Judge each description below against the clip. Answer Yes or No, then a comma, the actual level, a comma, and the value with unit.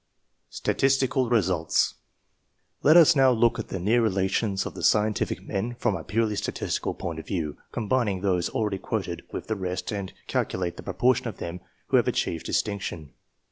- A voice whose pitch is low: Yes, low, 105 Hz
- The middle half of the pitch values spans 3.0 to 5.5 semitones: Yes, average, 4.3 semitones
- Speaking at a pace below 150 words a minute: No, average, 170 wpm